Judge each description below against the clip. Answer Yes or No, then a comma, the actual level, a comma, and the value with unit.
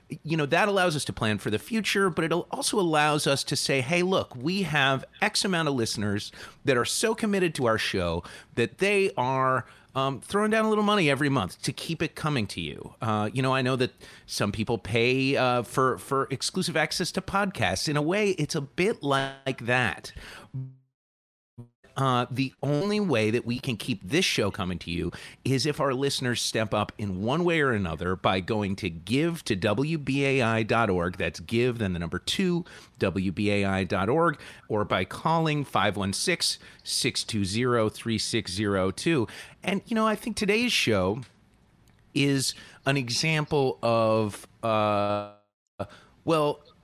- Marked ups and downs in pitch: Yes, wide, 6.7 semitones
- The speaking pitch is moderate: No, low, 130 Hz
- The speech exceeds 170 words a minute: No, average, 165 wpm